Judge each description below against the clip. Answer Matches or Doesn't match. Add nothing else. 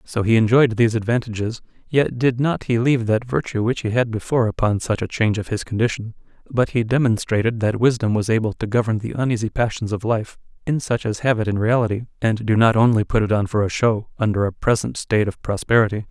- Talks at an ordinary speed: Doesn't match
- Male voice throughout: Matches